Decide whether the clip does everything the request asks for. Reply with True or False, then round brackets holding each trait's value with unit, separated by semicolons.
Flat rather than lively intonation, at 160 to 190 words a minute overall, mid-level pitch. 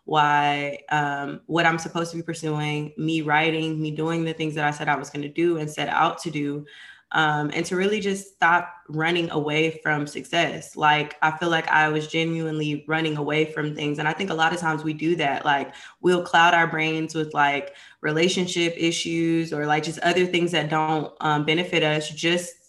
False (1.8 semitones; 205 wpm; 155 Hz)